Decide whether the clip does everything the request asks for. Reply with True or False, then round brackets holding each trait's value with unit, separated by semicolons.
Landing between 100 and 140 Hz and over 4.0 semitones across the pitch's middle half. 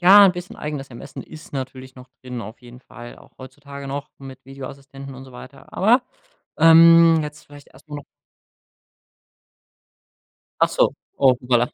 False (135 Hz; 2.7 semitones)